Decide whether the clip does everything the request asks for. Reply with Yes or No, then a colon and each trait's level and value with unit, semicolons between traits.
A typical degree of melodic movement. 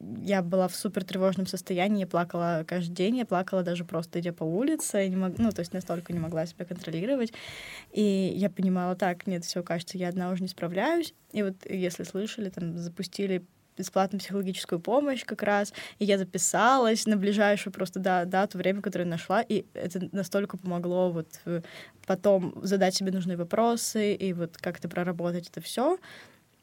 No: narrow, 2.2 semitones